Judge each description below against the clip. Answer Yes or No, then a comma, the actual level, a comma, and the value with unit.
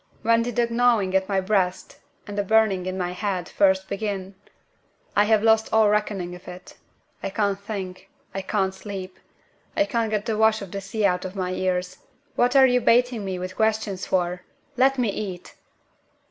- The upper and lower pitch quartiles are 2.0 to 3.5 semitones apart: Yes, average, 2.9 semitones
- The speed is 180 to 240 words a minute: Yes, average, 190 wpm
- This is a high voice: Yes, high, 200 Hz